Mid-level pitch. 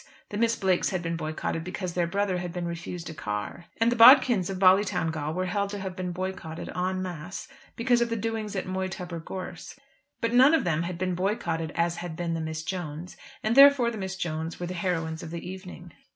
Yes: medium, 180 Hz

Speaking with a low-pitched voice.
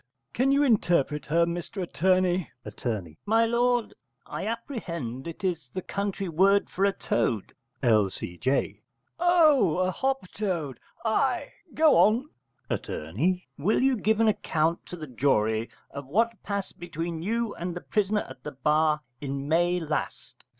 No: medium, 180 Hz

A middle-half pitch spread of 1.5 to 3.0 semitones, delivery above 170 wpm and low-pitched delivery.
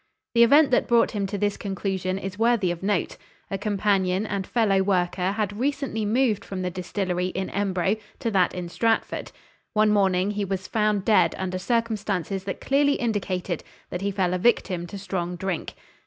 No: narrow, 2.6 semitones; average, 180 wpm; high, 195 Hz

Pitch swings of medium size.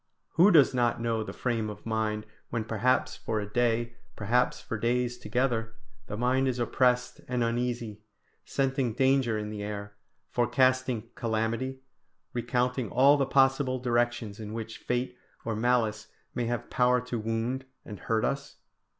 No: narrow, 2.1 semitones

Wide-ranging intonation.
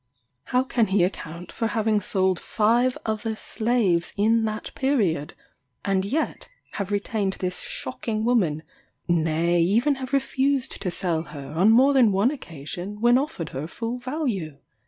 Yes: wide, 5.7 semitones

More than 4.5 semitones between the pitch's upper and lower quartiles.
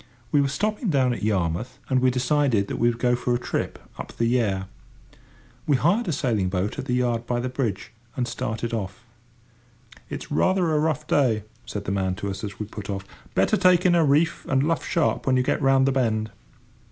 Yes: average, 5.0 semitones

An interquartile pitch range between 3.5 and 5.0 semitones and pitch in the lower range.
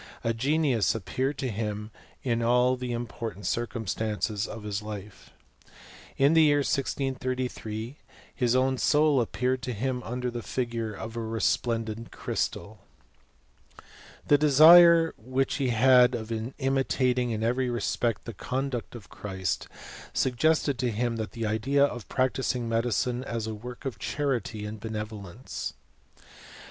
No: average, 2.9 semitones; low, 120 Hz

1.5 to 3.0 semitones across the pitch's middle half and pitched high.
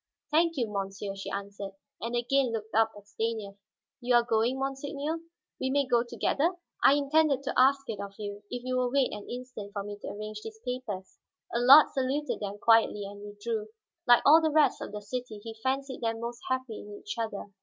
No: average, 4.4 semitones; high, 235 Hz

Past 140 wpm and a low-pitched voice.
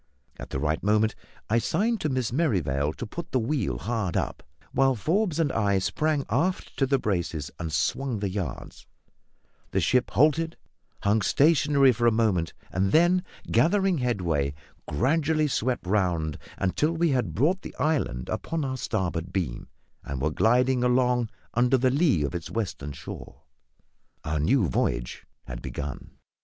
Yes: average, 155 wpm; low, 120 Hz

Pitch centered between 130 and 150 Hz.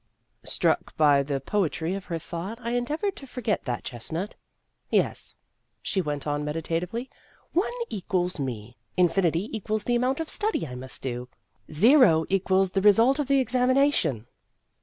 No: high, 190 Hz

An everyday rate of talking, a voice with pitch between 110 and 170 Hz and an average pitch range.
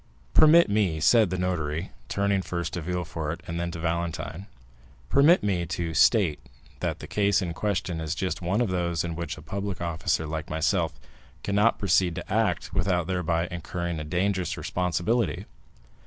No: average, 160 wpm; very low, 85 Hz; average, 3.3 semitones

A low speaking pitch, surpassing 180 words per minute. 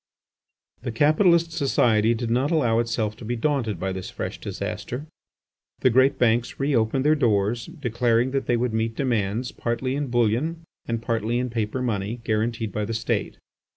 No: low, 120 Hz; average, 170 wpm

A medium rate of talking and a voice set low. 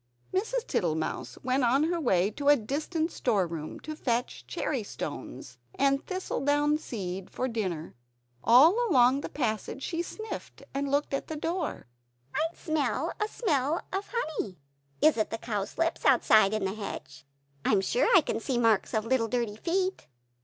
No: average, 165 wpm; very high, 260 Hz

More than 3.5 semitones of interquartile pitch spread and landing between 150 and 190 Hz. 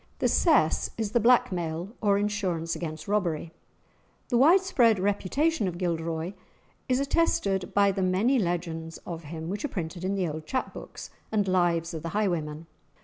Yes: average, 4.2 semitones; medium, 185 Hz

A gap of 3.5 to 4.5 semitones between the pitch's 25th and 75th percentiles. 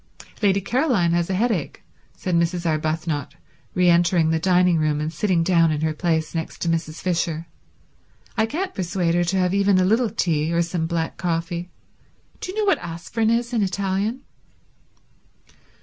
No: average, 3.1 semitones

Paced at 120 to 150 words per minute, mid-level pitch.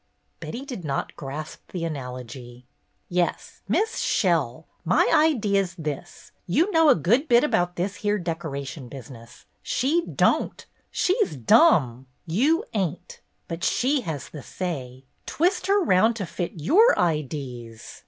Yes: average, 140 wpm; medium, 175 Hz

